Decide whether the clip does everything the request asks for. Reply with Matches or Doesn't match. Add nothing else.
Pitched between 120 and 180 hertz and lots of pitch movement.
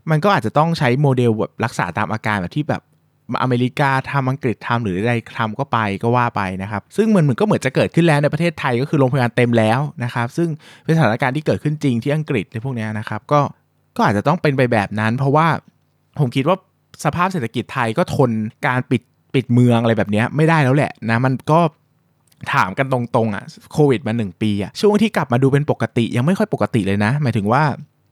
Doesn't match